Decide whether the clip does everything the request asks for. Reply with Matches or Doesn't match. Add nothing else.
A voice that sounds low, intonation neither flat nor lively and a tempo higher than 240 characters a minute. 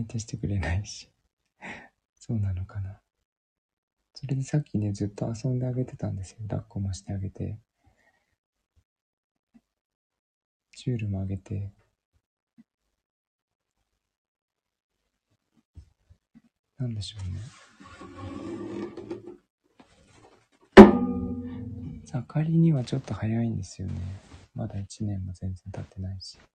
Doesn't match